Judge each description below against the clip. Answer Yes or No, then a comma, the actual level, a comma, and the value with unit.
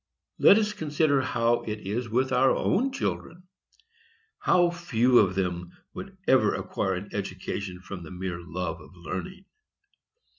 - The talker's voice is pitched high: No, low, 115 Hz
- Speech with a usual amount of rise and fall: No, wide, 9.0 semitones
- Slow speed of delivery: No, average, 145 wpm